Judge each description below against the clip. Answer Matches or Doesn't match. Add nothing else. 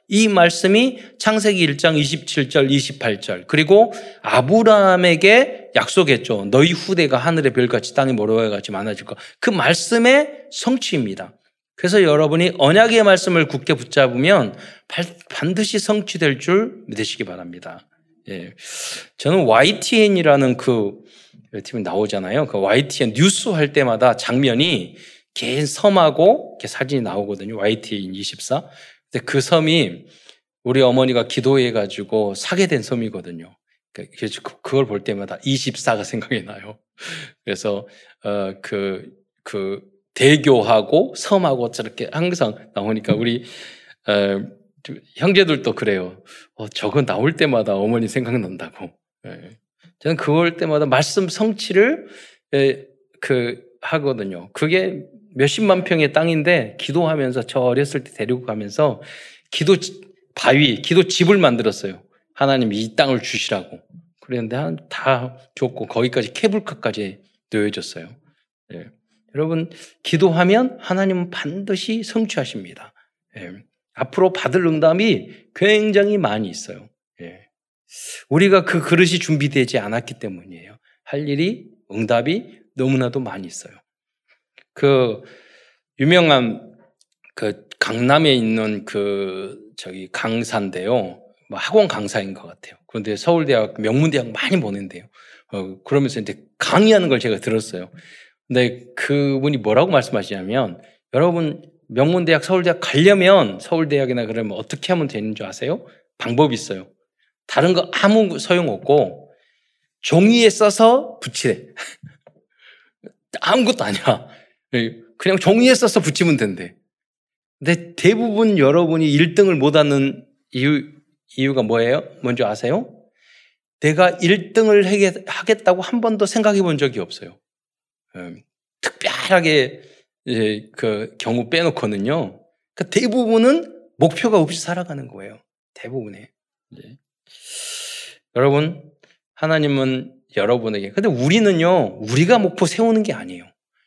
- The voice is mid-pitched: Matches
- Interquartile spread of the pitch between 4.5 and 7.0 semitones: Doesn't match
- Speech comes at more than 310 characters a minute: Doesn't match